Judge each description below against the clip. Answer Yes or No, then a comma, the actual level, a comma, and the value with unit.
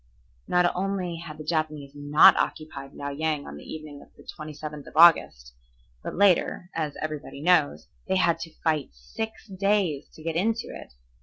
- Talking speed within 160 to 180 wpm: Yes, average, 170 wpm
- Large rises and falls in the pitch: No, average, 3.4 semitones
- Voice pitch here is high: No, medium, 155 Hz